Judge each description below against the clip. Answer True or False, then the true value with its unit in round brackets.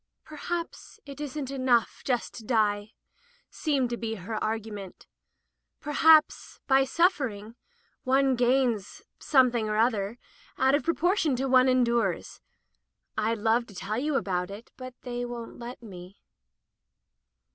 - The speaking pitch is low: False (245 Hz)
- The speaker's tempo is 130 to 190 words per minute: True (140 wpm)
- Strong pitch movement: False (3.7 semitones)